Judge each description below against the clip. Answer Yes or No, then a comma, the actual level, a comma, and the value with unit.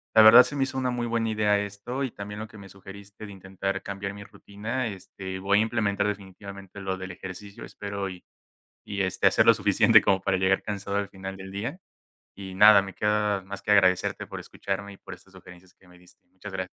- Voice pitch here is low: Yes, low, 100 Hz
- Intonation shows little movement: Yes, narrow, 1.5 semitones